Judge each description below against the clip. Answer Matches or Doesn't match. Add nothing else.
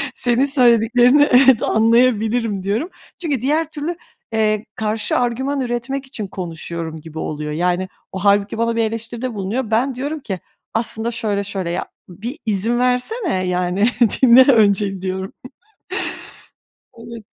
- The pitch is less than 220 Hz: Doesn't match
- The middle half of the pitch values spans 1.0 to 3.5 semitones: Doesn't match